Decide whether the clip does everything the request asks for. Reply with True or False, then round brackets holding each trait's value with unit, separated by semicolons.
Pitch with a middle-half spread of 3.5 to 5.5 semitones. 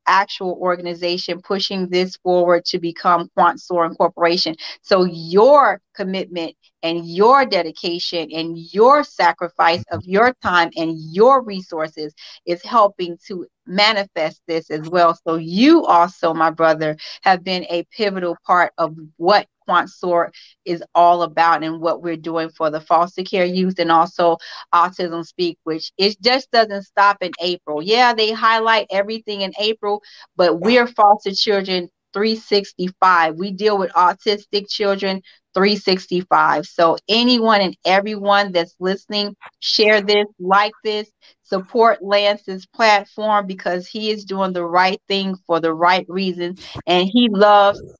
False (3.1 semitones)